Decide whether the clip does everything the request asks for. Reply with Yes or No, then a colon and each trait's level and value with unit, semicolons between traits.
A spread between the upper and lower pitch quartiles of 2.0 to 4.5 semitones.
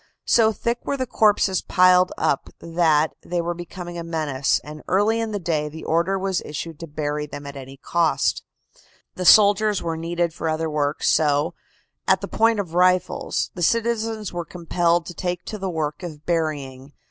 Yes: average, 3.6 semitones